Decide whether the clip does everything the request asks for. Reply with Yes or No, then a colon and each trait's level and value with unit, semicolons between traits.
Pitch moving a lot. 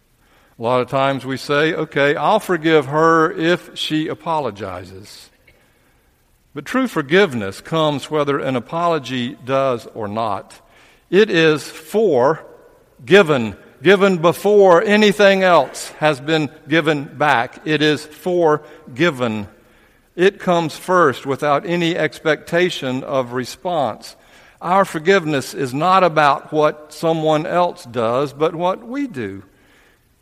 No: average, 4.2 semitones